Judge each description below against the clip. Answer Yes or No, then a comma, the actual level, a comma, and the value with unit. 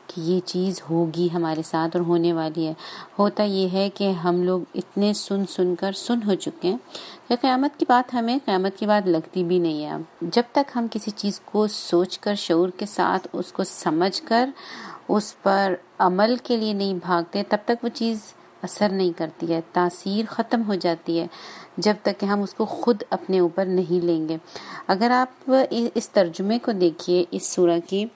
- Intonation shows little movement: No, average, 4.1 semitones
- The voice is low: No, high, 195 Hz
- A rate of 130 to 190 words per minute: No, average, 200 wpm